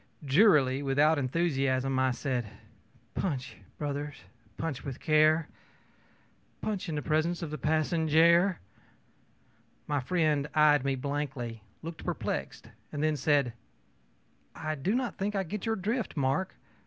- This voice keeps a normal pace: No, slow, 130 wpm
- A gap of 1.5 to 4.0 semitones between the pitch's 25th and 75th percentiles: Yes, average, 3.6 semitones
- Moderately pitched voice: Yes, medium, 150 Hz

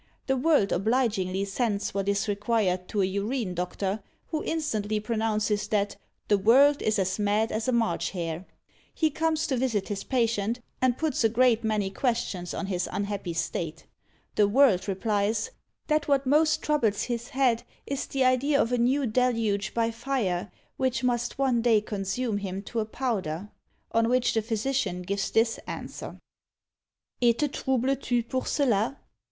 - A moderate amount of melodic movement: Yes, average, 4.2 semitones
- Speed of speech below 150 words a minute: No, average, 165 wpm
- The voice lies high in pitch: Yes, high, 225 Hz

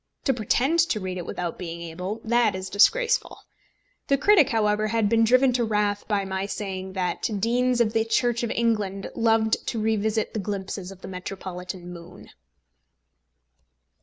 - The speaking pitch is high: Yes, high, 210 Hz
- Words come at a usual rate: Yes, average, 165 wpm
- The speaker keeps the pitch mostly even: No, average, 3.6 semitones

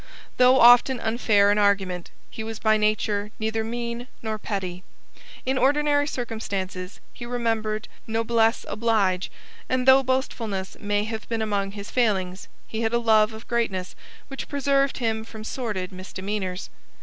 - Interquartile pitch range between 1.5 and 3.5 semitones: Yes, average, 2.9 semitones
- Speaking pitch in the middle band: No, high, 220 Hz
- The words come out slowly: No, average, 145 wpm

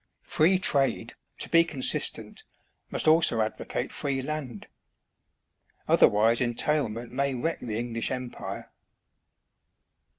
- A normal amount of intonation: Yes, average, 4.7 semitones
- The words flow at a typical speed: No, slow, 100 wpm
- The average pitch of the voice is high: No, low, 130 Hz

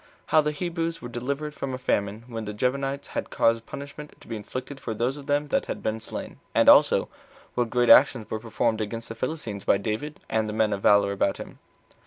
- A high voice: No, low, 120 Hz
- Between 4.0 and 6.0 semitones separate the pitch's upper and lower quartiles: Yes, average, 4.3 semitones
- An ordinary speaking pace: No, fast, 220 wpm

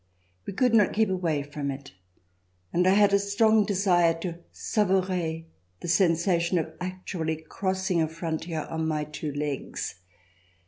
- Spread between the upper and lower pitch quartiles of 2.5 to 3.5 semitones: Yes, average, 3.2 semitones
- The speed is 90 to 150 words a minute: Yes, average, 145 wpm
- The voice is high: No, medium, 175 Hz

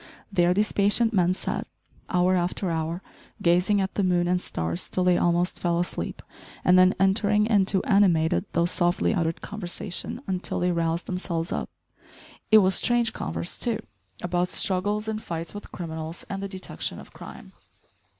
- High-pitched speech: No, medium, 180 Hz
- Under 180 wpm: Yes, average, 160 wpm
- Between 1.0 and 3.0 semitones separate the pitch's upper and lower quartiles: Yes, narrow, 2.6 semitones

